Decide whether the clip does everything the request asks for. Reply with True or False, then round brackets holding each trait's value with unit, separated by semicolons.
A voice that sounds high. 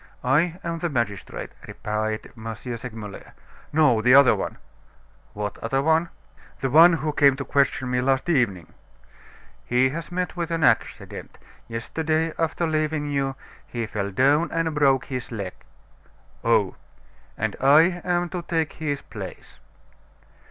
False (140 Hz)